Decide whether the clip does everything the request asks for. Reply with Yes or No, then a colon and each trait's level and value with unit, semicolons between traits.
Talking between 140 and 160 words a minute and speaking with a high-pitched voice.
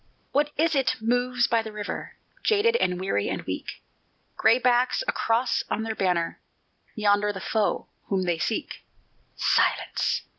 Yes: average, 150 wpm; high, 225 Hz